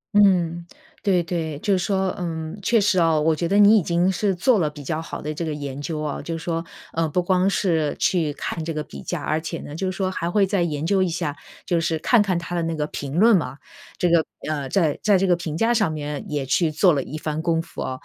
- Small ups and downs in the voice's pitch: No, average, 3.3 semitones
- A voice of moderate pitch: Yes, medium, 170 Hz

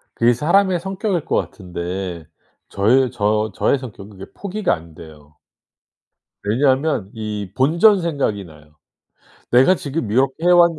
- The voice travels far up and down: Yes, wide, 8.9 semitones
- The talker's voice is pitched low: Yes, low, 120 Hz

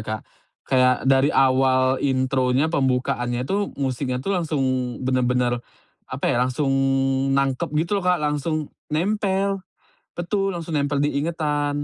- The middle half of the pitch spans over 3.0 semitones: Yes, average, 4.0 semitones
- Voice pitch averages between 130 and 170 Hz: Yes, medium, 140 Hz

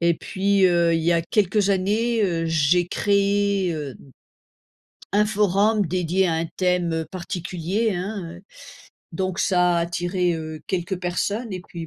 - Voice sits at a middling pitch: Yes, medium, 180 Hz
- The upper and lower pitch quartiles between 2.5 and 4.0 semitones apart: Yes, average, 2.9 semitones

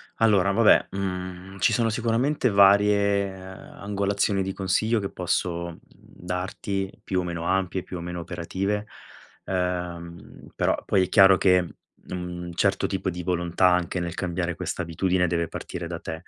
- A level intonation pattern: Yes, narrow, 2.0 semitones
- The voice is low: Yes, very low, 95 Hz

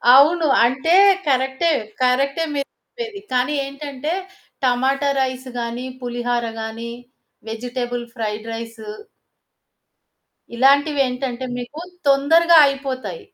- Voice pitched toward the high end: Yes, very high, 260 Hz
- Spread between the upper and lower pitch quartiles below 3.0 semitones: Yes, narrow, 2.6 semitones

